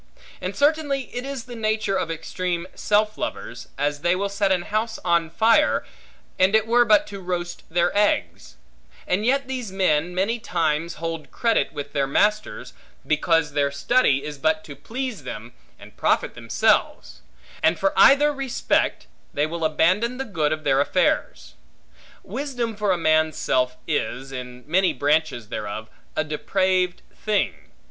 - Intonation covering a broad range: Yes, wide, 6.3 semitones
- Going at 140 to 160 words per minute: Yes, average, 155 wpm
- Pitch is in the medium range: Yes, medium, 180 Hz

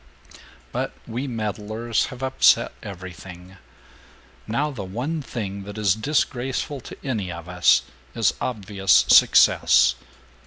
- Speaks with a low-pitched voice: Yes, low, 110 Hz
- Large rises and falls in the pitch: No, average, 4.9 semitones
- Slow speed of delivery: Yes, slow, 115 wpm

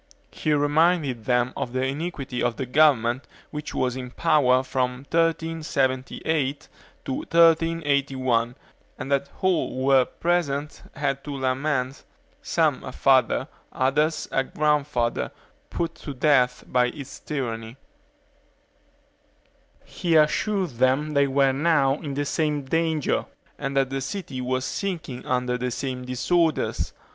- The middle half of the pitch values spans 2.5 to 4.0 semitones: Yes, average, 3.1 semitones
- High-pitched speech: No, medium, 140 Hz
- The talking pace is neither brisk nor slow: No, slow, 130 wpm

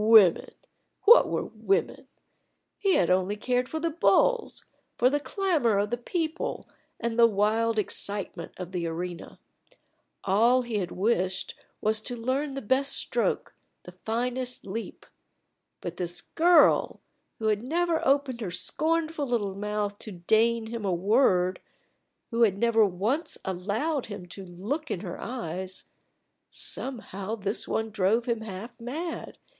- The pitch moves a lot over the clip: No, average, 5.0 semitones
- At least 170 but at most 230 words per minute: No, average, 145 wpm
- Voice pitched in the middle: No, high, 225 Hz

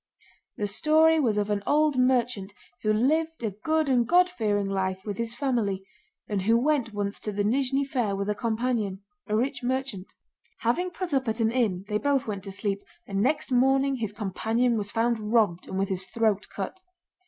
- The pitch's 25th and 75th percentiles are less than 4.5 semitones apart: No, average, 4.8 semitones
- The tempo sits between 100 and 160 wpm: No, average, 190 wpm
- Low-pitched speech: No, high, 225 Hz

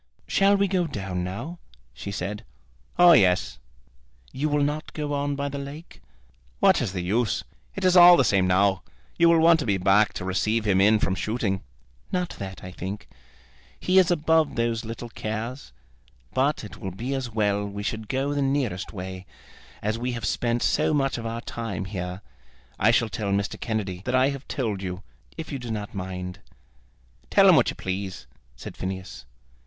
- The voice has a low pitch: Yes, low, 110 Hz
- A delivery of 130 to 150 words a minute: No, average, 190 wpm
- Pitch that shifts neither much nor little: No, wide, 6.5 semitones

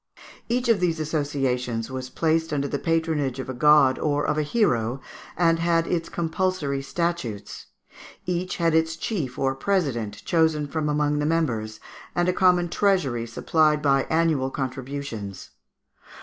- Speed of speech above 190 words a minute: No, average, 150 wpm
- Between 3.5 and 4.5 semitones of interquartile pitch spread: Yes, average, 4.0 semitones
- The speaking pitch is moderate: Yes, medium, 150 Hz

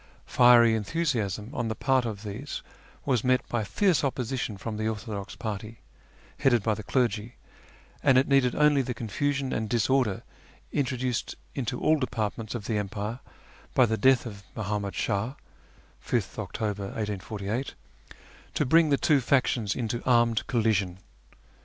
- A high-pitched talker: No, low, 115 Hz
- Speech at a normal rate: Yes, average, 145 wpm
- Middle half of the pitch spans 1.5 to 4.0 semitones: Yes, average, 3.5 semitones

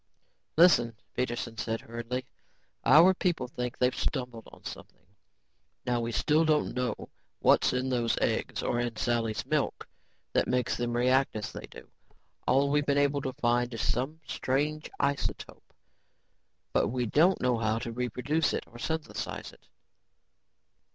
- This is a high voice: No, low, 125 Hz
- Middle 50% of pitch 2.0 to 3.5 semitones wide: Yes, average, 3.2 semitones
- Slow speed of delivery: No, average, 150 wpm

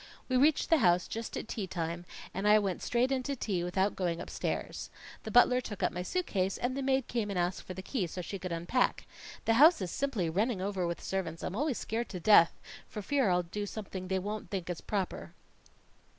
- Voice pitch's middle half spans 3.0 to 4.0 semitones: No, average, 5.0 semitones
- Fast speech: Yes, fast, 230 wpm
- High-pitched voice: Yes, high, 200 Hz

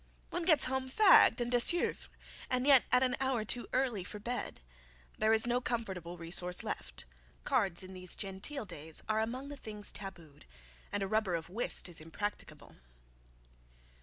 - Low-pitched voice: No, high, 220 Hz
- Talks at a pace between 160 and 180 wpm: Yes, average, 165 wpm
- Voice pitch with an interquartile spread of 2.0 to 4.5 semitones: No, wide, 5.4 semitones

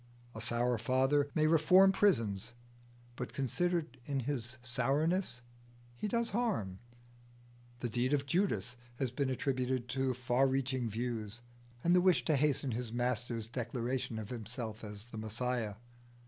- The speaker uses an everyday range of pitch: Yes, average, 3.4 semitones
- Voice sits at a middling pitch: No, low, 125 Hz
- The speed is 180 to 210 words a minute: No, average, 140 wpm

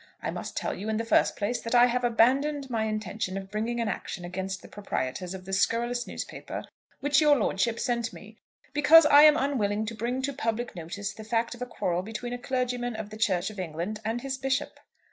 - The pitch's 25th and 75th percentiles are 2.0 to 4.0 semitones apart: Yes, average, 3.5 semitones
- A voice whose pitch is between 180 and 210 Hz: No, high, 230 Hz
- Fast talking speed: Yes, fast, 220 wpm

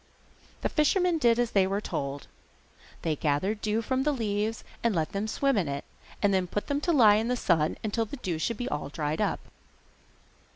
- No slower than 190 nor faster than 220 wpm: Yes, average, 200 wpm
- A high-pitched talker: Yes, high, 210 Hz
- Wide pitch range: Yes, wide, 6.1 semitones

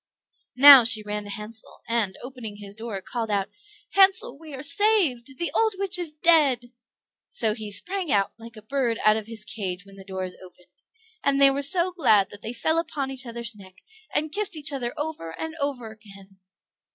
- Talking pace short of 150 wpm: No, average, 200 wpm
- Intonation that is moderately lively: No, wide, 6.3 semitones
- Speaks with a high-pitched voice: Yes, high, 235 Hz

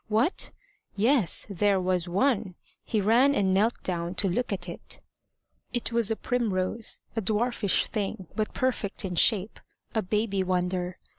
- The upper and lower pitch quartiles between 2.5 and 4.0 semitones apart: Yes, average, 3.6 semitones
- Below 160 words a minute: Yes, average, 150 wpm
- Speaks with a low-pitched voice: No, high, 205 Hz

